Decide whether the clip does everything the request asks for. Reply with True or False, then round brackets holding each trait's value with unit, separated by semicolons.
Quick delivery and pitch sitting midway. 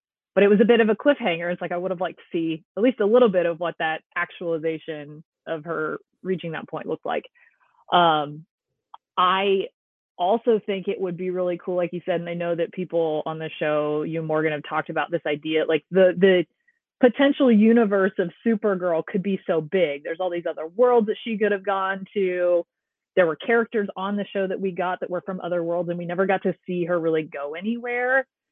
True (225 wpm; 180 Hz)